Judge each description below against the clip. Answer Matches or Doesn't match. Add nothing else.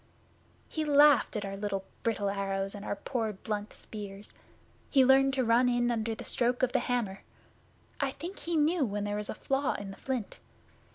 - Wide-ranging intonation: Doesn't match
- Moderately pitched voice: Doesn't match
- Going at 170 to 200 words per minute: Matches